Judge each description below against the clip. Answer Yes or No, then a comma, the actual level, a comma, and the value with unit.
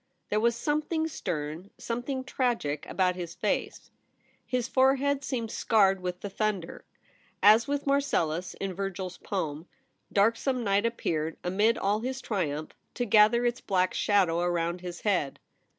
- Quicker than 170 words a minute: No, average, 145 wpm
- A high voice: Yes, high, 205 Hz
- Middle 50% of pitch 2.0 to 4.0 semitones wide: No, wide, 5.4 semitones